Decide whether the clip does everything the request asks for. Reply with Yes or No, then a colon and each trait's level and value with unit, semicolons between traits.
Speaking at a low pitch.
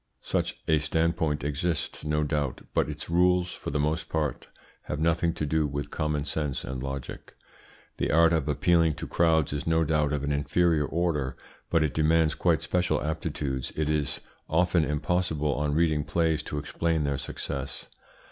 Yes: very low, 75 Hz